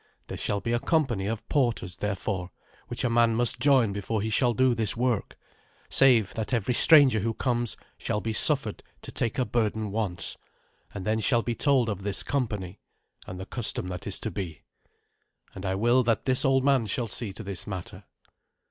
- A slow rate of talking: No, average, 195 wpm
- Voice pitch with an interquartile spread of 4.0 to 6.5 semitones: No, average, 3.5 semitones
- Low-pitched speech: Yes, low, 115 Hz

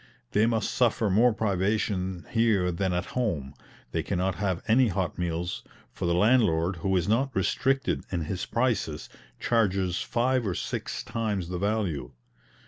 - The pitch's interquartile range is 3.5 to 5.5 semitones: Yes, average, 4.3 semitones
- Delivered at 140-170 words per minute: Yes, average, 150 wpm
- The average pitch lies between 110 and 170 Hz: No, very low, 95 Hz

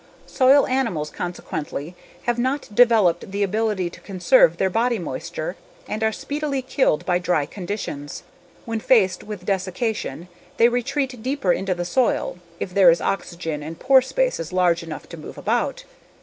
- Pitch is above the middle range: Yes, high, 195 Hz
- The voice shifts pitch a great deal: Yes, wide, 5.9 semitones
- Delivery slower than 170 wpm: Yes, average, 155 wpm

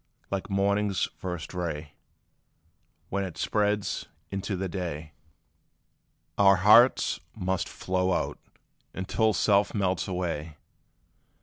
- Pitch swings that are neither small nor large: No, narrow, 2.1 semitones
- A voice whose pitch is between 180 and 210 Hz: No, very low, 95 Hz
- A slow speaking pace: Yes, slow, 95 wpm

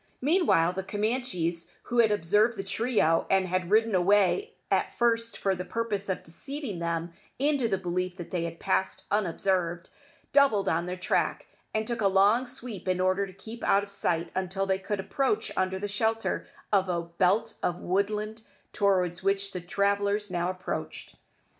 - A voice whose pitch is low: No, high, 195 Hz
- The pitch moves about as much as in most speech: Yes, average, 3.2 semitones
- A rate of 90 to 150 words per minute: No, average, 170 wpm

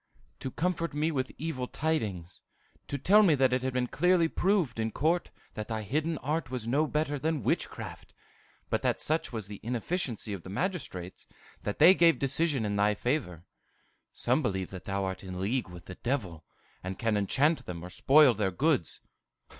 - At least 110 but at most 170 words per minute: No, average, 185 wpm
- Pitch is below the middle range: Yes, low, 130 Hz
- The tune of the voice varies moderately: No, wide, 7.6 semitones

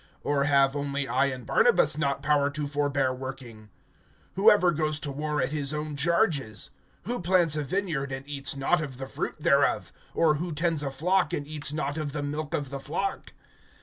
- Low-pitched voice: No, medium, 145 Hz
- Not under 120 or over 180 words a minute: No, average, 195 wpm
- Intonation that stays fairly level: Yes, narrow, 2.1 semitones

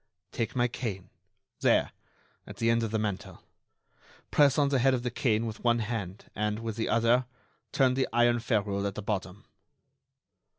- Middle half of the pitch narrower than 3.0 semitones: Yes, narrow, 2.5 semitones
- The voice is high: No, low, 115 Hz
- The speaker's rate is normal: Yes, average, 175 wpm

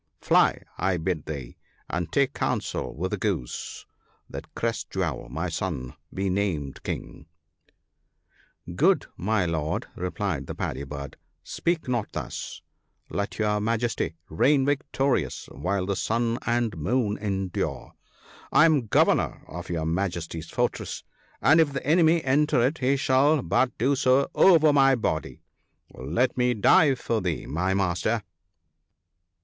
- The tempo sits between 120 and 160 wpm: Yes, average, 145 wpm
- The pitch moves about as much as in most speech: No, wide, 7.5 semitones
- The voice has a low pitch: Yes, low, 105 Hz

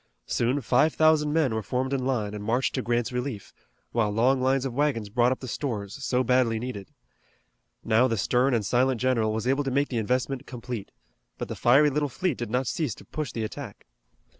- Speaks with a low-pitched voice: Yes, low, 125 Hz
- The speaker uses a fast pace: Yes, fast, 210 wpm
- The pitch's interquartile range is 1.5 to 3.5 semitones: Yes, average, 3.0 semitones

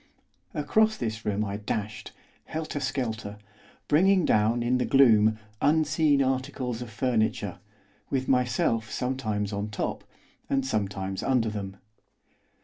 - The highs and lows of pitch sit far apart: No, average, 4.1 semitones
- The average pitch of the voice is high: No, low, 120 Hz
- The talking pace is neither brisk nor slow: No, slow, 120 wpm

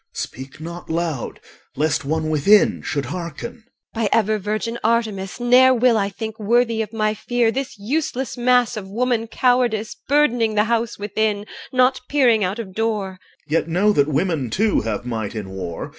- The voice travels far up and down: Yes, wide, 5.8 semitones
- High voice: Yes, high, 215 Hz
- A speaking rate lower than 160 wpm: No, average, 175 wpm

